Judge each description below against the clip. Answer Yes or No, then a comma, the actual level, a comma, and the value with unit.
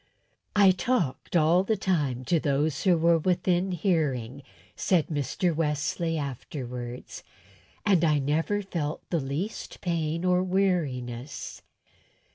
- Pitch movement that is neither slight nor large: Yes, average, 4.3 semitones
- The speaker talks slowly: Yes, slow, 115 wpm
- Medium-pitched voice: Yes, medium, 165 Hz